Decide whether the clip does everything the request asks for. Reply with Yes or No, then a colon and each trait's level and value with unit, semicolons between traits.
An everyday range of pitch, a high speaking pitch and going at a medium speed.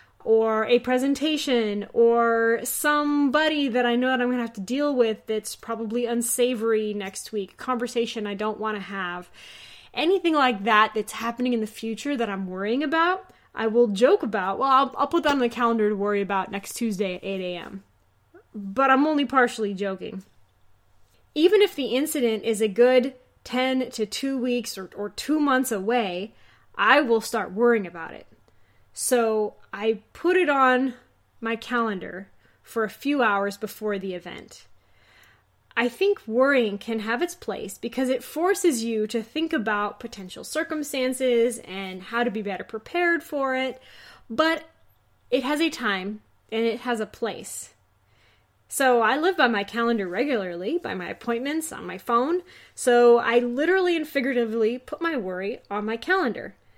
Yes: average, 4.1 semitones; high, 235 Hz; average, 165 wpm